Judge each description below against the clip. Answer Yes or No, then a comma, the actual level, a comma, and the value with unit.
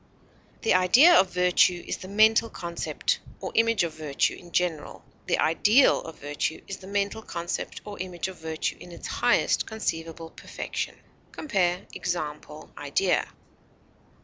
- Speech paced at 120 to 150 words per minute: Yes, average, 145 wpm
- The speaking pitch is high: No, medium, 180 Hz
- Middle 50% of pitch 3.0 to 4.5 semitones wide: Yes, average, 3.8 semitones